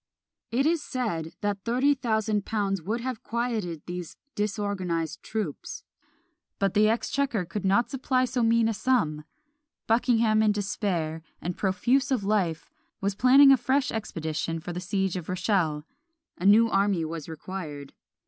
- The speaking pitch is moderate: No, high, 205 Hz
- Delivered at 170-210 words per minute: No, average, 150 wpm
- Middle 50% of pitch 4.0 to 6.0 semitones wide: Yes, average, 4.8 semitones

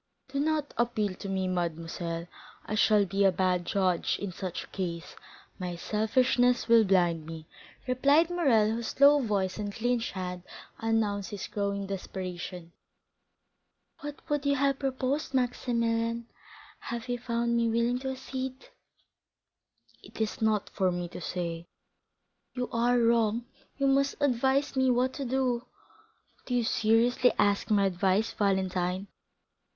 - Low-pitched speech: No, high, 225 Hz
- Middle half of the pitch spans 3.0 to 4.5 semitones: No, average, 5.1 semitones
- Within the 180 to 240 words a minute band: No, average, 140 wpm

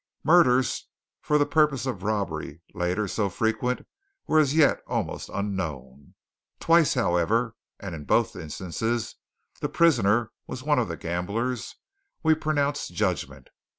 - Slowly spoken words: Yes, slow, 130 wpm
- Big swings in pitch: Yes, wide, 7.8 semitones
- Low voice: Yes, low, 110 Hz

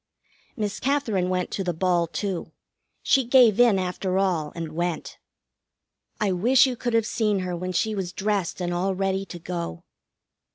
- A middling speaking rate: Yes, average, 170 wpm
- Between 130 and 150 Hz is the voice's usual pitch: No, high, 190 Hz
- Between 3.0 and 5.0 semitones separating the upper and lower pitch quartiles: Yes, average, 3.4 semitones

